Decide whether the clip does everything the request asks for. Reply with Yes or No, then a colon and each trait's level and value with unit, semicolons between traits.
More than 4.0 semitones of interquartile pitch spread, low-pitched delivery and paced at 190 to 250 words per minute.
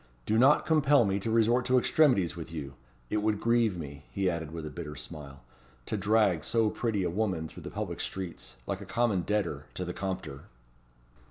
Yes: wide, 5.5 semitones; very low, 95 Hz; average, 195 wpm